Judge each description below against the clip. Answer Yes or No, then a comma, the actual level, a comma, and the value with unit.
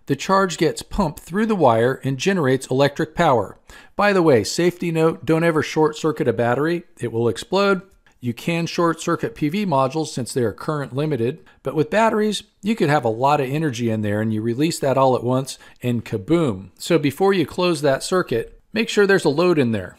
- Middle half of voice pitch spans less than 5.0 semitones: No, wide, 5.4 semitones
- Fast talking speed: Yes, fast, 210 wpm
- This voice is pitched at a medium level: Yes, medium, 155 Hz